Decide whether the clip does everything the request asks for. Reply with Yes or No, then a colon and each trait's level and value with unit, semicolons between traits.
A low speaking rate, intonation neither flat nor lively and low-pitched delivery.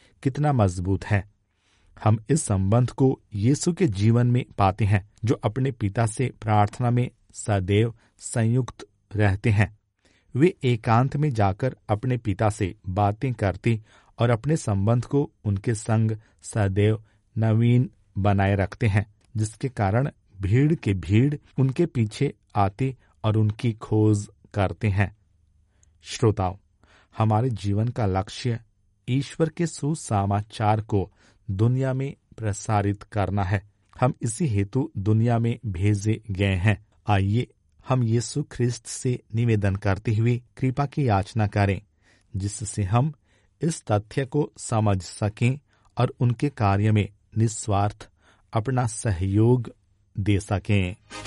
No: average, 125 wpm; average, 3.4 semitones; low, 110 Hz